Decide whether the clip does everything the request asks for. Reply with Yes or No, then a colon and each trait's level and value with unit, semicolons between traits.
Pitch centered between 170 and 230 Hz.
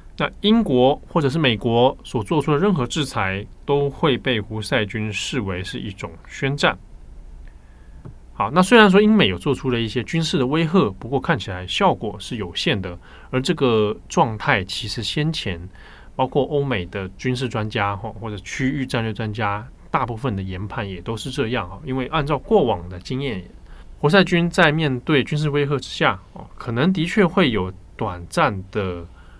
No: low, 125 Hz